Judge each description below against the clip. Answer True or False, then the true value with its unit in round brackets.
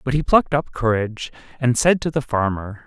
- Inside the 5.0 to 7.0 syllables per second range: True (5.7 syllables/s)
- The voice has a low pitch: True (130 Hz)